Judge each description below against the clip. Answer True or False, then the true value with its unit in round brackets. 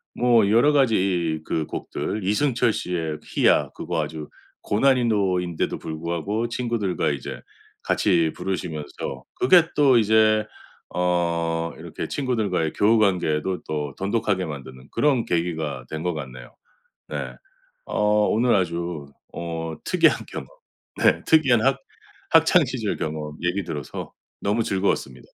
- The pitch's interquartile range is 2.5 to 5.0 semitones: False (5.5 semitones)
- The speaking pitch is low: True (90 Hz)